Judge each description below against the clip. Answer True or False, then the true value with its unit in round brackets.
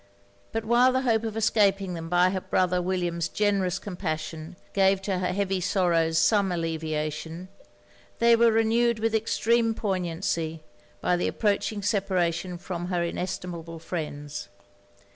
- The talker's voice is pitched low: False (185 Hz)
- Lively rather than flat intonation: False (3.9 semitones)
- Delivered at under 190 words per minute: True (135 wpm)